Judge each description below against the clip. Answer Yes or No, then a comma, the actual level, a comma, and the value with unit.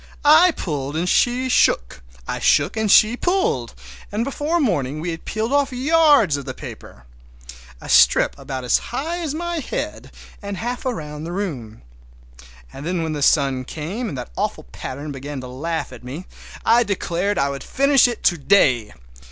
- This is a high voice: No, medium, 175 Hz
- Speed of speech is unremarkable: Yes, average, 175 wpm